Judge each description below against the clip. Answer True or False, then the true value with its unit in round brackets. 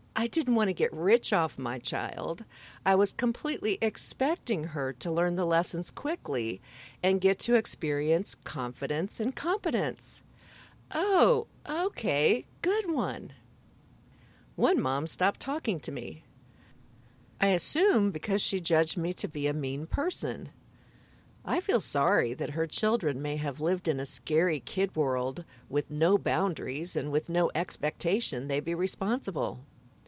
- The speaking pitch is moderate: True (170 Hz)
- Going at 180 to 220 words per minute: False (140 wpm)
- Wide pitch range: True (7.7 semitones)